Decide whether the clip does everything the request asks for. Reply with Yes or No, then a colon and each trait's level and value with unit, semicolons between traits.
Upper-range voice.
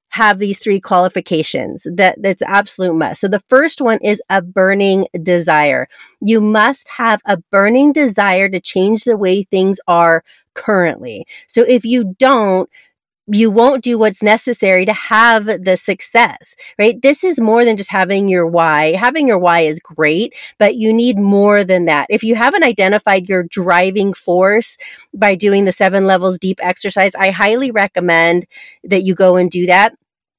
Yes: high, 200 Hz